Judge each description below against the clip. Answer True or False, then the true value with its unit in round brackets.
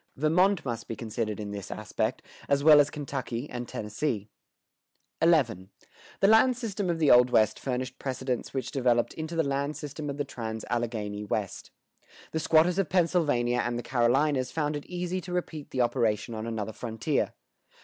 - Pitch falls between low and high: False (130 Hz)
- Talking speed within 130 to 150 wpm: False (170 wpm)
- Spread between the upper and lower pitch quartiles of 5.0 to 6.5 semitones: True (5.3 semitones)